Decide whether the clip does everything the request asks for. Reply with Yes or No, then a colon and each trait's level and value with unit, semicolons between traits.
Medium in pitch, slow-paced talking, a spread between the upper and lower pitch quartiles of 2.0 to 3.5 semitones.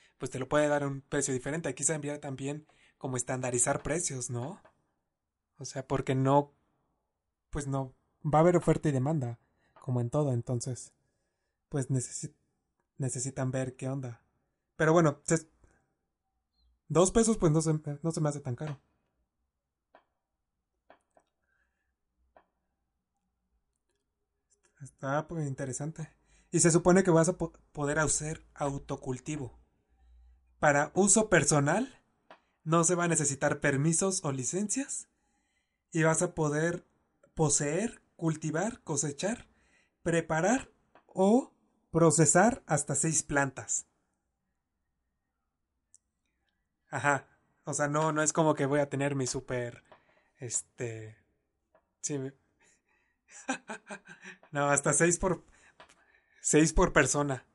No: medium, 145 Hz; slow, 120 wpm; average, 4.3 semitones